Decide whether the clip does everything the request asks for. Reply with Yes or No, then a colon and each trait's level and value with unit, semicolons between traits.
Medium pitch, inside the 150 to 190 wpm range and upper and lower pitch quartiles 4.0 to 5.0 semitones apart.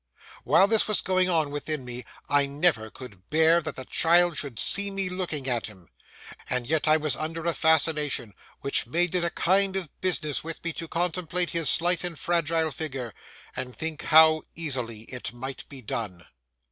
Yes: medium, 155 Hz; average, 185 wpm; average, 4.7 semitones